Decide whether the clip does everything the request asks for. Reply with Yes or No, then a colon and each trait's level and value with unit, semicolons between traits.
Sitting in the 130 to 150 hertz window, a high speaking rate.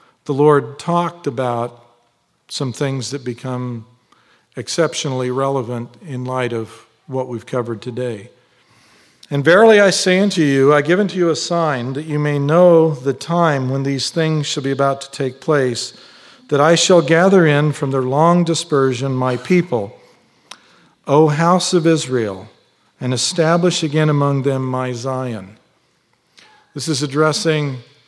No: medium, 140 Hz; average, 145 wpm